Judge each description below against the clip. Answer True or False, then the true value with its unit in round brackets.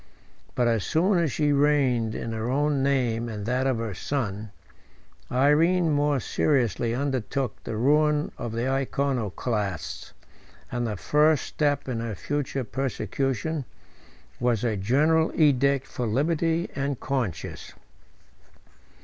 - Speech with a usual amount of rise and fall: True (4.1 semitones)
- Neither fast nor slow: False (125 wpm)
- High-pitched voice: False (135 Hz)